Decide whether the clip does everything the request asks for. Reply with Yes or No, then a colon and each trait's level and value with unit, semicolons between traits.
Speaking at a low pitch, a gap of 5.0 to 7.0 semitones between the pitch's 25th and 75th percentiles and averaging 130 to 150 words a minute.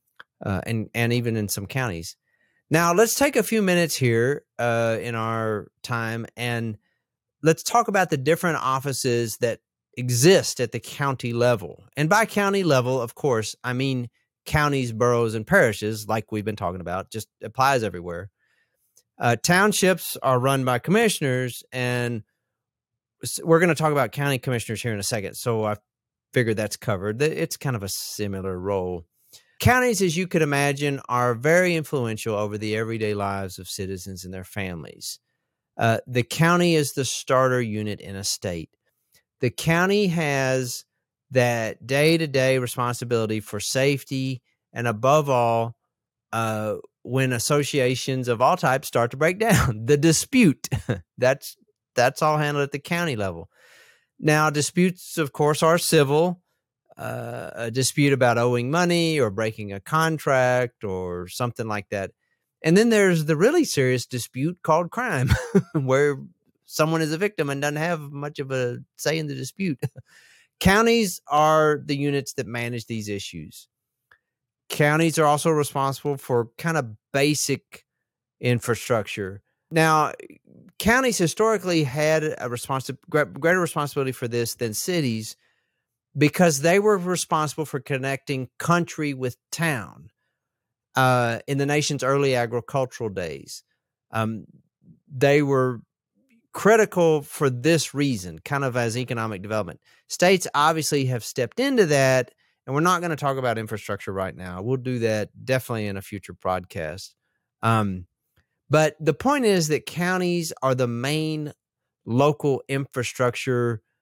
Yes: low, 130 Hz; average, 5.3 semitones; average, 145 wpm